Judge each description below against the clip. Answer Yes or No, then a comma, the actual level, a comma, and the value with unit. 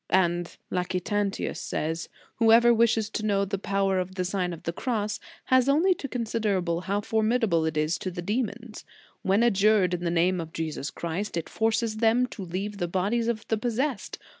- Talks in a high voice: Yes, high, 200 Hz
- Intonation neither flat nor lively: Yes, average, 4.1 semitones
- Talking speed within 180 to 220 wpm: Yes, average, 190 wpm